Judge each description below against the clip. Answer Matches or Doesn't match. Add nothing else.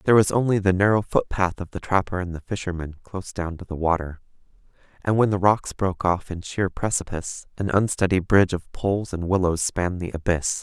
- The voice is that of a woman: Doesn't match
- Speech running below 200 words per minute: Doesn't match